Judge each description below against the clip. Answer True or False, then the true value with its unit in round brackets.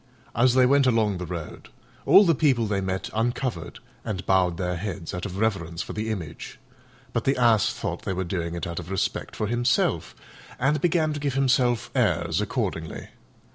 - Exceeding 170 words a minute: True (185 wpm)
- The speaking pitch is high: False (105 Hz)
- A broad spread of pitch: True (5.9 semitones)